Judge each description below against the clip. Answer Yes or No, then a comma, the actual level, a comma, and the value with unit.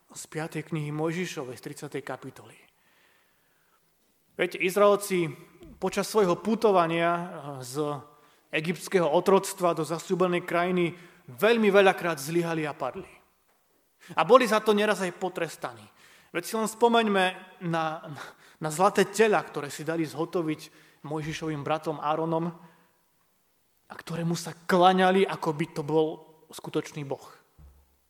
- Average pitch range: Yes, average, 3.1 semitones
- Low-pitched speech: No, medium, 165 Hz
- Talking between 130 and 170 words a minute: No, average, 115 wpm